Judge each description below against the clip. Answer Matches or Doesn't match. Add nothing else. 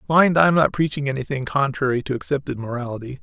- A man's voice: Matches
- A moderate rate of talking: Matches